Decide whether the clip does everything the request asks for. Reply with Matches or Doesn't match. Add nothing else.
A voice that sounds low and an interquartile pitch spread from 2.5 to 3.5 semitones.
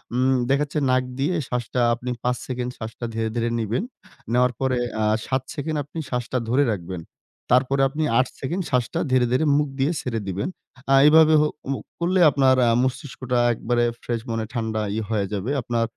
Matches